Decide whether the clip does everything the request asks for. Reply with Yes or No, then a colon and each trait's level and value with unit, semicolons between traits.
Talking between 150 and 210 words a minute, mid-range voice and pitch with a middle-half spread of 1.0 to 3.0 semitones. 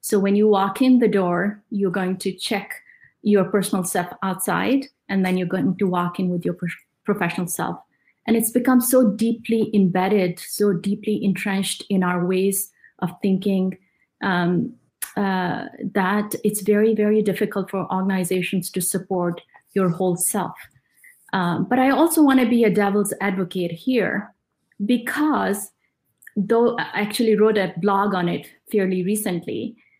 No: average, 155 wpm; high, 200 Hz; average, 2.7 semitones